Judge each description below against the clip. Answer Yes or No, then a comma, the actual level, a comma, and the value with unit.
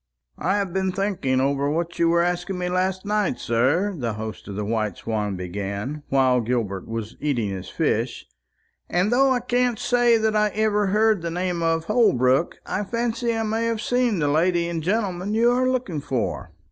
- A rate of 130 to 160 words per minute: No, average, 190 wpm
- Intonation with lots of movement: Yes, wide, 8.7 semitones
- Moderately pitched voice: Yes, medium, 175 Hz